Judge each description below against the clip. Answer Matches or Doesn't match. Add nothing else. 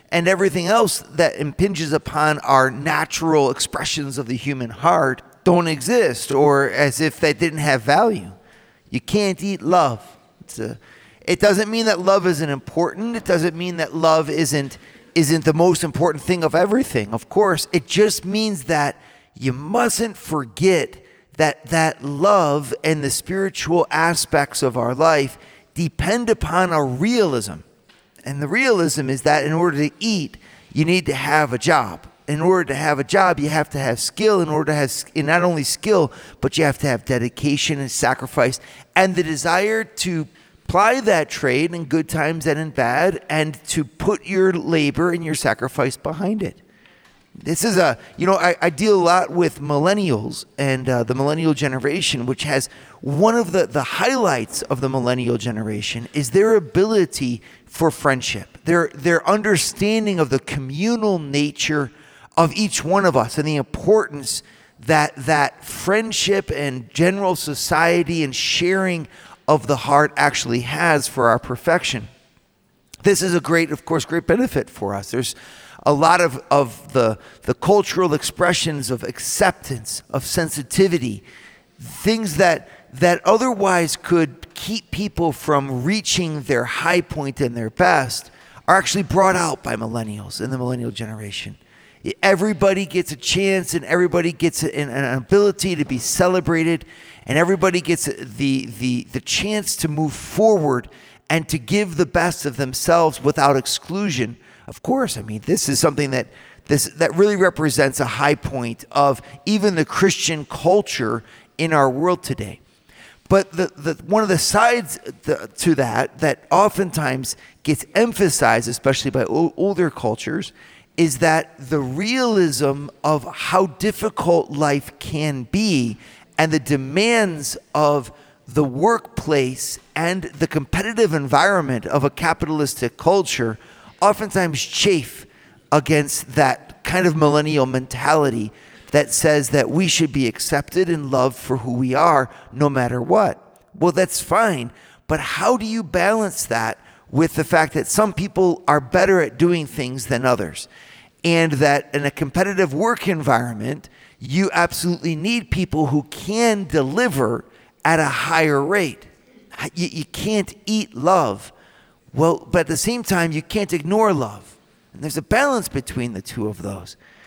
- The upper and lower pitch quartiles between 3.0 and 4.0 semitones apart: Doesn't match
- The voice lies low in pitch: Doesn't match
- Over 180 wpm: Doesn't match